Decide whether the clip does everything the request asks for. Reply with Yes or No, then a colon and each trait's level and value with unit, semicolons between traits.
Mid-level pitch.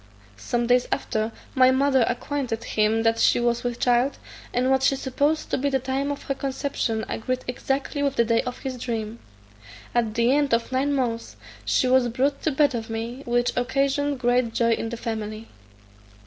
No: very high, 250 Hz